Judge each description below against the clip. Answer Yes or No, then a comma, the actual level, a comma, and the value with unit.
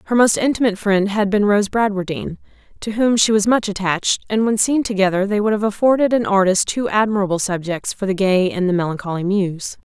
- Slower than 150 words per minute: No, fast, 205 wpm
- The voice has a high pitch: Yes, high, 205 Hz